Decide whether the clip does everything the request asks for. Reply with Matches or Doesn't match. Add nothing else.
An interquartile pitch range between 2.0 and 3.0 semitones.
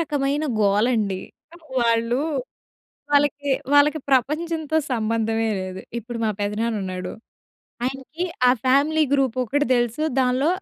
Doesn't match